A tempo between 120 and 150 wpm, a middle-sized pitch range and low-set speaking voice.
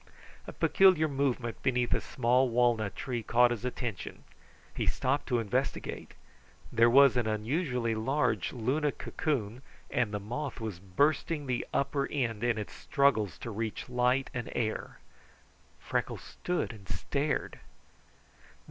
Yes: slow, 135 wpm; average, 3.6 semitones; low, 125 Hz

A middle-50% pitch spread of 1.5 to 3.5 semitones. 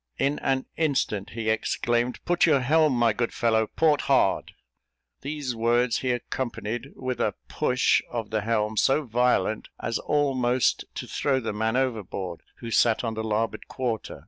Yes: average, 3.0 semitones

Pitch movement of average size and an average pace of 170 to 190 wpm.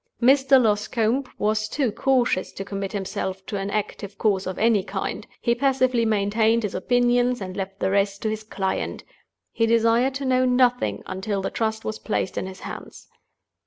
Yes: average, 3.7 semitones; average, 175 wpm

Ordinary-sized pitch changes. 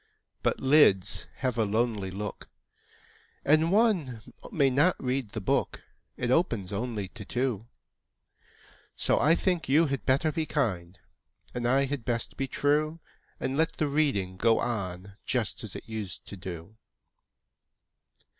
No: wide, 6.0 semitones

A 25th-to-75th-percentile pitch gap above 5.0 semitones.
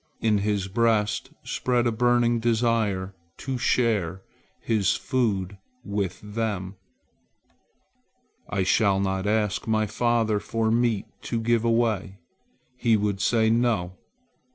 No: average, 2.9 semitones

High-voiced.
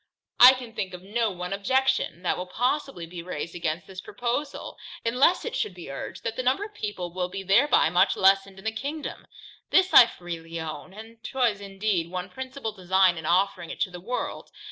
Yes: high, 195 Hz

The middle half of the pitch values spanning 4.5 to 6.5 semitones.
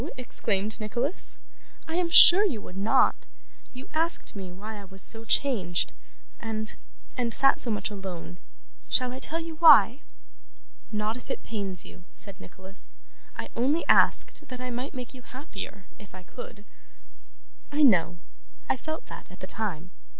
Yes: average, 5.2 semitones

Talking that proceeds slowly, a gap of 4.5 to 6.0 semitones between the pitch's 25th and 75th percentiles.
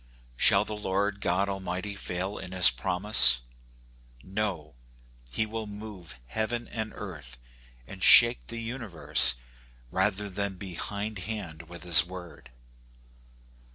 No: slow, 120 wpm; average, 3.2 semitones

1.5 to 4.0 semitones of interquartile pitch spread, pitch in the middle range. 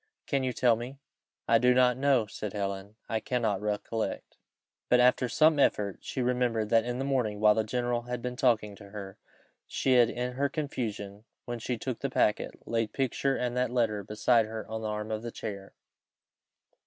No: average, 2.8 semitones; low, 115 Hz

